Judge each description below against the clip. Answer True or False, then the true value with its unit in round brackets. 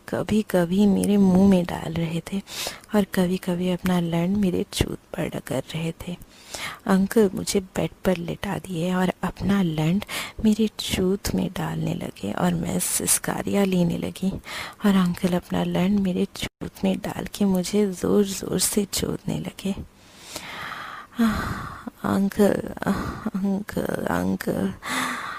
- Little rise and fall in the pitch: True (2.2 semitones)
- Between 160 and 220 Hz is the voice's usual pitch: True (190 Hz)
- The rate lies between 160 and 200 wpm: False (130 wpm)